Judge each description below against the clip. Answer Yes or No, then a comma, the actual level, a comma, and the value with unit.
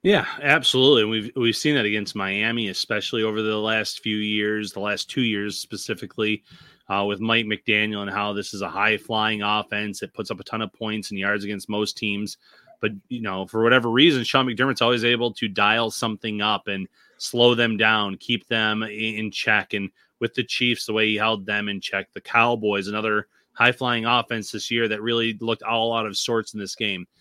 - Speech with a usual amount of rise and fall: No, narrow, 2.0 semitones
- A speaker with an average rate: No, fast, 210 wpm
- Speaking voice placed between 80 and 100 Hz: No, low, 110 Hz